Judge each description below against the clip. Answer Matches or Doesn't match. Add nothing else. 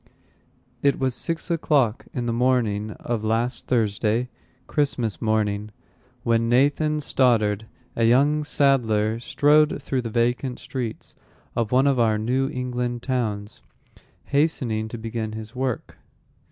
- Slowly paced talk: Matches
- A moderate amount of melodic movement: Matches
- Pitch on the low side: Matches